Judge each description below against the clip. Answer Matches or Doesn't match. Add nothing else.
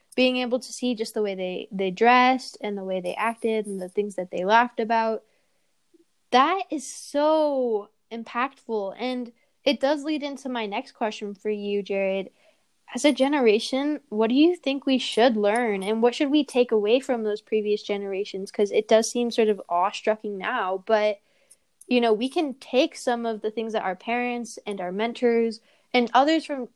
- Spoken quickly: Doesn't match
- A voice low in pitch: Doesn't match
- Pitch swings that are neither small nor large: Matches